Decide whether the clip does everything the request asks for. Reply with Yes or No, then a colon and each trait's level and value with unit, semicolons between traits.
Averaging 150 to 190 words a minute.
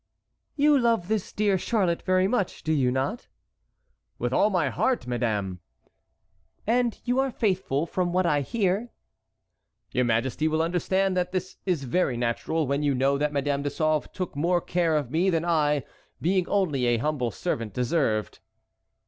Yes: average, 165 wpm